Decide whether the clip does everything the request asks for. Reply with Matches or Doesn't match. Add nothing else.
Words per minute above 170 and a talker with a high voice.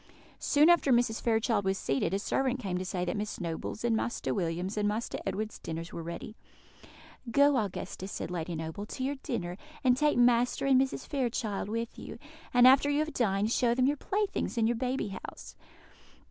Matches